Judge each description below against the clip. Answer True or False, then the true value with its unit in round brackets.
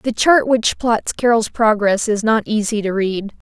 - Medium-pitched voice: False (220 Hz)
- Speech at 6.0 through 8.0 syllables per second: False (4.2 syllables/s)